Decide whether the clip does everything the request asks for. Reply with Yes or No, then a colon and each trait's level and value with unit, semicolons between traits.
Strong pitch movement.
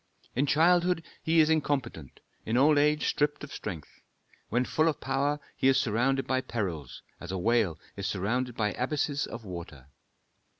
Yes: wide, 6.2 semitones